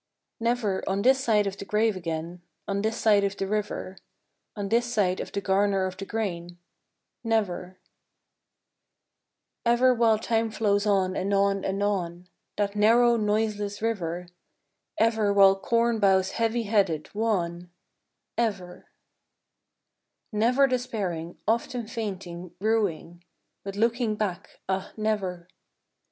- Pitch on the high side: Yes, high, 205 Hz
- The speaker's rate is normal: No, slow, 130 wpm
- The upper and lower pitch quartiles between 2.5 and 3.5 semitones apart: Yes, average, 3.0 semitones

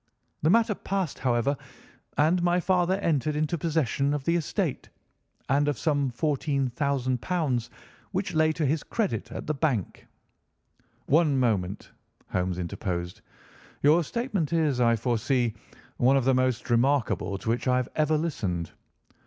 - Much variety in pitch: No, average, 4.8 semitones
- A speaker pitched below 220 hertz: Yes, medium, 140 Hz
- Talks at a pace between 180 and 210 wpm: No, average, 145 wpm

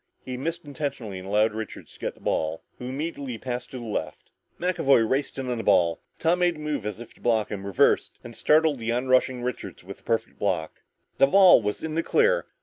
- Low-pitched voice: Yes, low, 125 Hz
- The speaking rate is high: Yes, fast, 225 wpm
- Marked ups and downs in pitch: Yes, wide, 5.8 semitones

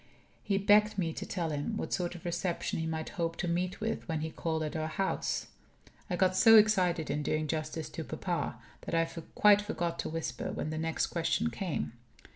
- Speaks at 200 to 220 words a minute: Yes, fast, 205 wpm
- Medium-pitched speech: Yes, medium, 170 Hz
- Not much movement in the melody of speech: No, average, 3.4 semitones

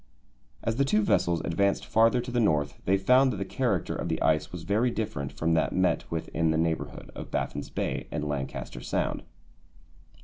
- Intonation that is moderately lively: No, wide, 5.9 semitones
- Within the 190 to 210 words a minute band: Yes, average, 195 wpm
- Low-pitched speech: Yes, very low, 90 Hz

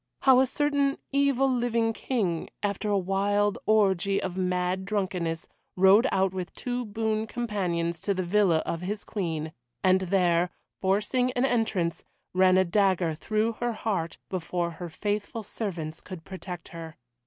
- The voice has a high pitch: Yes, high, 195 Hz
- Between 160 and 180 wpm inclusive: No, average, 150 wpm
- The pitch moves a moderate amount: Yes, average, 3.7 semitones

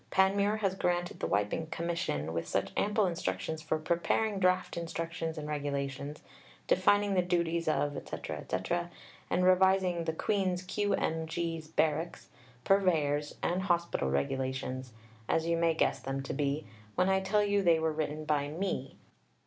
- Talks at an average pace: Yes, average, 150 wpm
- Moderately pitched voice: Yes, medium, 165 Hz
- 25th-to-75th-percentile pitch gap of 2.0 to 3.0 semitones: No, average, 3.7 semitones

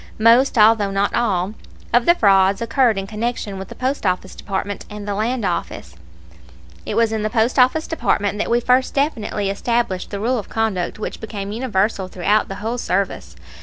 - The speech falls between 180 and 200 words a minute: Yes, average, 185 wpm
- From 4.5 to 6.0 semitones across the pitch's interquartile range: No, average, 3.2 semitones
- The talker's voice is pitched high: Yes, high, 215 Hz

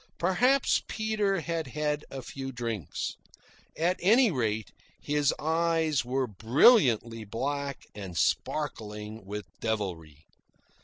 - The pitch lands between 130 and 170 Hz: Yes, low, 135 Hz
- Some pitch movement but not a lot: No, wide, 7.0 semitones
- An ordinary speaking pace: No, slow, 105 wpm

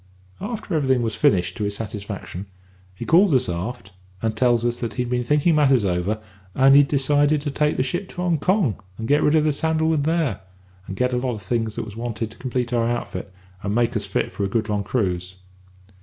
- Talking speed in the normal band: No, fast, 225 wpm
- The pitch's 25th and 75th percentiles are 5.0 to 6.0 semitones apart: Yes, wide, 5.5 semitones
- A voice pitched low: Yes, low, 120 Hz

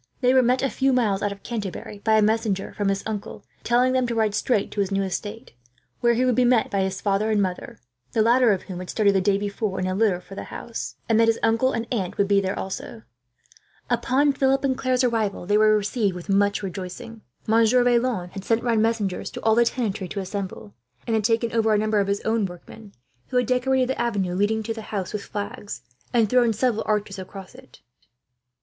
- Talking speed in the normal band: No, fast, 225 wpm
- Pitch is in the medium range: No, high, 215 Hz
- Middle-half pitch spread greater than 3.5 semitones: No, average, 3.1 semitones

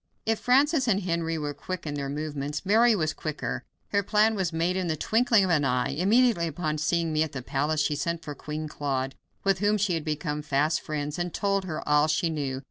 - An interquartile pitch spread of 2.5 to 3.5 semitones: No, average, 4.7 semitones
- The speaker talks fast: Yes, fast, 220 wpm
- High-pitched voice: No, medium, 160 Hz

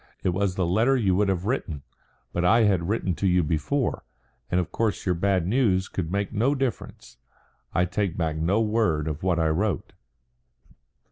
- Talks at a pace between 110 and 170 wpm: No, average, 185 wpm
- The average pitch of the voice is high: No, very low, 95 Hz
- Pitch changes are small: No, average, 4.0 semitones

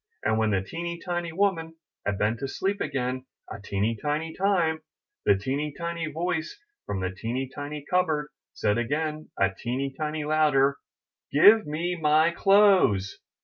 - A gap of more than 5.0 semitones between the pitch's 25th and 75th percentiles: Yes, wide, 5.4 semitones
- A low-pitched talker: No, medium, 150 Hz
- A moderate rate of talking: Yes, average, 155 wpm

